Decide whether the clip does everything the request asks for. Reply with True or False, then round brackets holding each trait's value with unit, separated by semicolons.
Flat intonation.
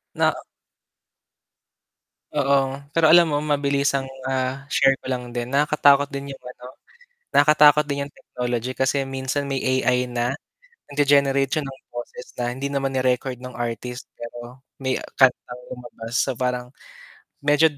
True (2.1 semitones)